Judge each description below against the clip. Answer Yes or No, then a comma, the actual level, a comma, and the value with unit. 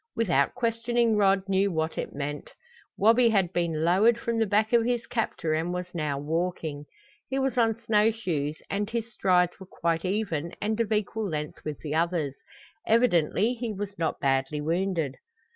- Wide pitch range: Yes, wide, 5.7 semitones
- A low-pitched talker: No, high, 190 Hz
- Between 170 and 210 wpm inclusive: Yes, average, 175 wpm